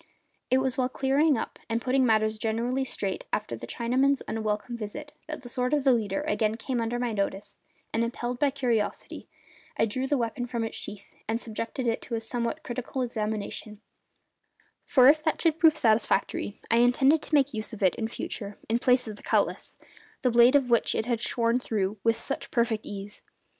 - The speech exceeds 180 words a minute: Yes, average, 195 wpm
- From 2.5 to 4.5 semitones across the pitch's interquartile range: Yes, average, 3.0 semitones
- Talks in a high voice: Yes, high, 235 Hz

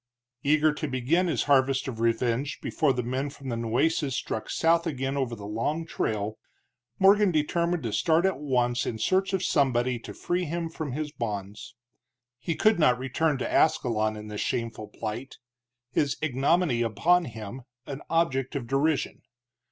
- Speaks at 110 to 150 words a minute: No, average, 165 wpm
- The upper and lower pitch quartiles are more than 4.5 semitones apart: Yes, average, 5.3 semitones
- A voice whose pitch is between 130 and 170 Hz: Yes, low, 135 Hz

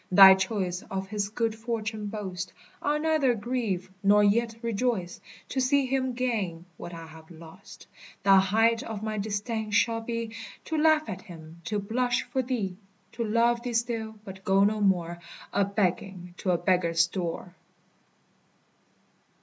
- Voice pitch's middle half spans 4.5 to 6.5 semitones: No, average, 3.8 semitones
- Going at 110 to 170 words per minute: Yes, average, 160 wpm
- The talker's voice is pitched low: No, high, 210 Hz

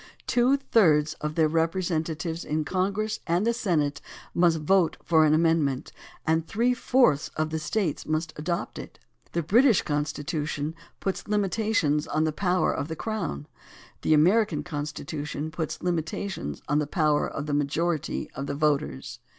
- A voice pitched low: No, medium, 160 Hz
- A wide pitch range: No, average, 3.7 semitones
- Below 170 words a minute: Yes, average, 155 wpm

